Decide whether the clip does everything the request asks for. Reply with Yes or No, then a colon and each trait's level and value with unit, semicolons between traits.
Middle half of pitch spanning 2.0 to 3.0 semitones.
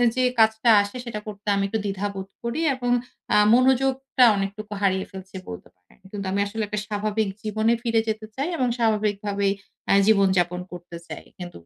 Yes: narrow, 2.6 semitones